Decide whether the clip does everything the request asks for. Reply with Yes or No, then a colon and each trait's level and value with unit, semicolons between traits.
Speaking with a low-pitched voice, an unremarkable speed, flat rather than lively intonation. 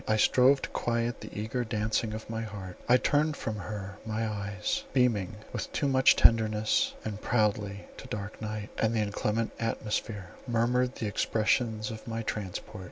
Yes: low, 110 Hz; average, 165 wpm; narrow, 1.8 semitones